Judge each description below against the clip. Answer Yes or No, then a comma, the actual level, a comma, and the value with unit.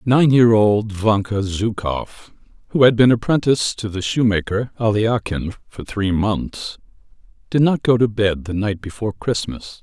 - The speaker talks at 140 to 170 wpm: Yes, average, 155 wpm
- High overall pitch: No, low, 110 Hz